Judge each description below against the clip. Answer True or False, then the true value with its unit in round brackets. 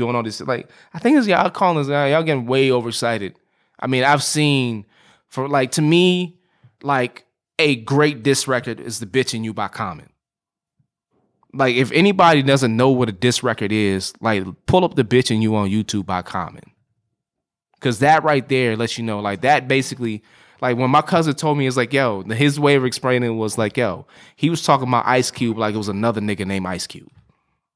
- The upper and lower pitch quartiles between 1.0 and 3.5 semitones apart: False (4.3 semitones)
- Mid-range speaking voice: False (125 Hz)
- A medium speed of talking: False (210 wpm)